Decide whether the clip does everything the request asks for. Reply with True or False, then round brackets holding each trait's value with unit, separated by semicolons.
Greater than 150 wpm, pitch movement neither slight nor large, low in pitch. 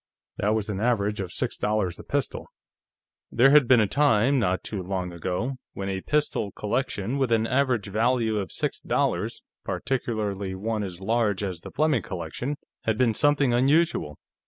True (170 wpm; 4.7 semitones; 110 Hz)